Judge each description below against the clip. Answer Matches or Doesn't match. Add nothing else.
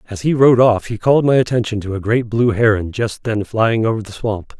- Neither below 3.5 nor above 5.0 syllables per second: Doesn't match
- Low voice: Matches